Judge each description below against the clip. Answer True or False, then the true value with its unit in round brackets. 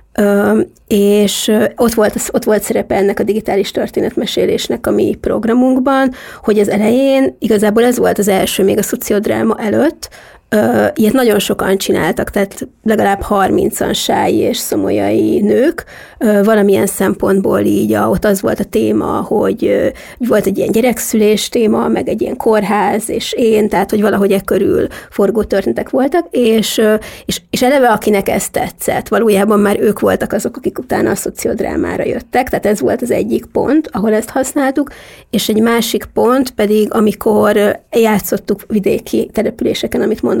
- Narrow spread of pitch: True (2.3 semitones)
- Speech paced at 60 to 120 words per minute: False (155 wpm)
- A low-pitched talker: False (215 Hz)